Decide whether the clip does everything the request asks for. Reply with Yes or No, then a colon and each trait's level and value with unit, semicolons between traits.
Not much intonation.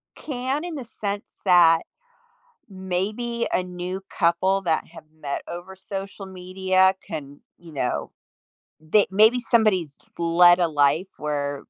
No: average, 3.3 semitones